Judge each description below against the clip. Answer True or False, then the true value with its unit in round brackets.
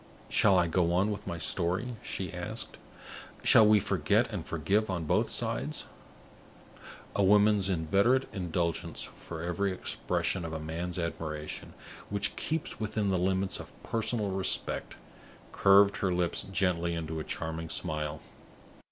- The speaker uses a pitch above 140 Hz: False (90 Hz)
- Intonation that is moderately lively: True (3.4 semitones)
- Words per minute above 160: False (140 wpm)